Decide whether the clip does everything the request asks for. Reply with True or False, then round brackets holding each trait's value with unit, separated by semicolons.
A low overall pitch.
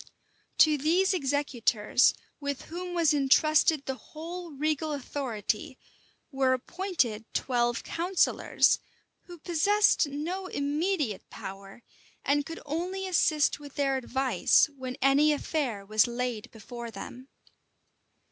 False (285 Hz)